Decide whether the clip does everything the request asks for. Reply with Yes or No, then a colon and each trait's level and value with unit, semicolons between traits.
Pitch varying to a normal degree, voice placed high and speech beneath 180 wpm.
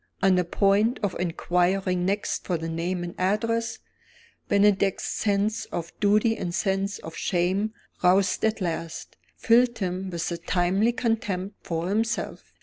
Yes: average, 3.1 semitones; high, 195 Hz; average, 145 wpm